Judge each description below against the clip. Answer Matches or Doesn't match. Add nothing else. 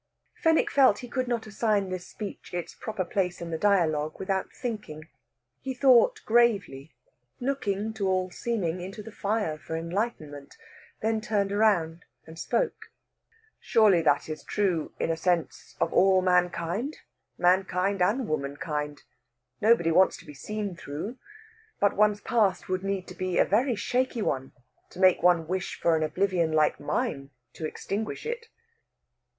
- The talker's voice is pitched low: Doesn't match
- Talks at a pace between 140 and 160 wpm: Matches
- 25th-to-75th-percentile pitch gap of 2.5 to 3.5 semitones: Doesn't match